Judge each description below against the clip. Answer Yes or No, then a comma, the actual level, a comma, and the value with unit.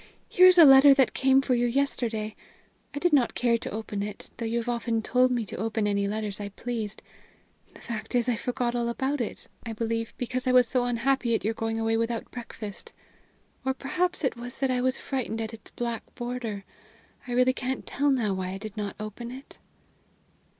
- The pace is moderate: No, fast, 210 wpm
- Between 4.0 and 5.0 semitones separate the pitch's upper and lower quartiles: No, narrow, 2.5 semitones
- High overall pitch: Yes, high, 235 Hz